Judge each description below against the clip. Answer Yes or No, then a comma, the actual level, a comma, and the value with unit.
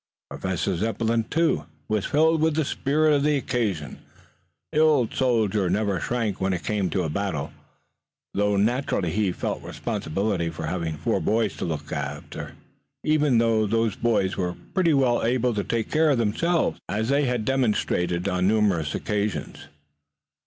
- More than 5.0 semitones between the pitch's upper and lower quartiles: Yes, wide, 5.5 semitones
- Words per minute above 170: No, average, 160 wpm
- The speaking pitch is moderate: No, low, 110 Hz